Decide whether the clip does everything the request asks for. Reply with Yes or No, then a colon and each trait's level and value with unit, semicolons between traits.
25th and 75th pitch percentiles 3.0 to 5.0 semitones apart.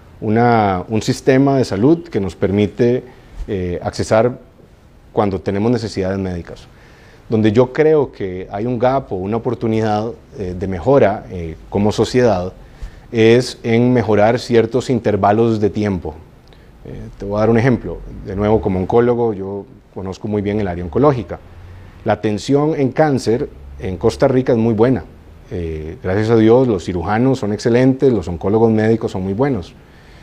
Yes: average, 4.1 semitones